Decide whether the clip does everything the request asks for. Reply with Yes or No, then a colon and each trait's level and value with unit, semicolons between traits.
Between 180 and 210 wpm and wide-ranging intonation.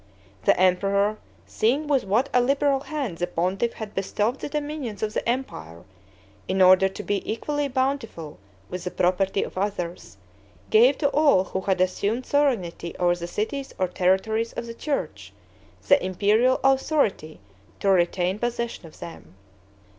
No: average, 155 wpm; wide, 6.1 semitones